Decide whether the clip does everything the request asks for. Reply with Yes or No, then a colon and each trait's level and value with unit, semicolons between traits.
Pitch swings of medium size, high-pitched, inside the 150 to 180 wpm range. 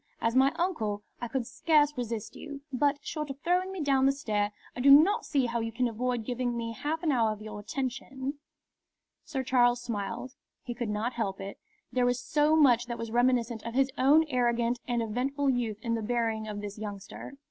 No: average, 3.3 semitones; high, 245 Hz; fast, 205 wpm